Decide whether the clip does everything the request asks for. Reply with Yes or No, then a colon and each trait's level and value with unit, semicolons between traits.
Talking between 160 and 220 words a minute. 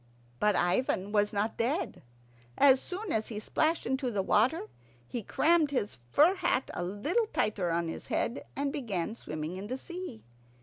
Yes: average, 170 wpm